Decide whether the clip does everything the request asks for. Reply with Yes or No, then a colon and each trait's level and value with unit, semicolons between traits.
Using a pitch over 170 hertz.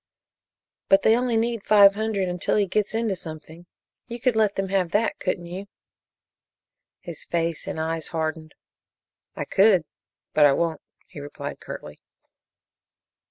Yes: high, 190 Hz